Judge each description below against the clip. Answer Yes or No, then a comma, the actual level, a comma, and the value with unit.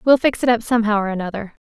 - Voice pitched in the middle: No, high, 220 Hz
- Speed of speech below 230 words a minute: No, fast, 245 wpm